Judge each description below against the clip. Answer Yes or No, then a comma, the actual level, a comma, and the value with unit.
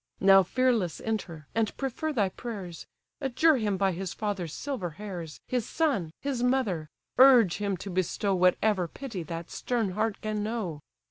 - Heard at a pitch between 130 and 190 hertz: No, high, 205 Hz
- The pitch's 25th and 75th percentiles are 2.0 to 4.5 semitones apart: No, average, 5.0 semitones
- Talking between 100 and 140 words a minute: No, average, 155 wpm